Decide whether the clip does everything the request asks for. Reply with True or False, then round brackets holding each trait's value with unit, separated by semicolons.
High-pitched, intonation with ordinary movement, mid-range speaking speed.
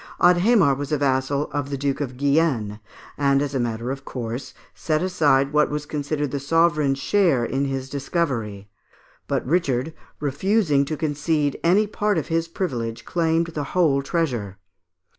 False (145 Hz; 3.6 semitones; 160 wpm)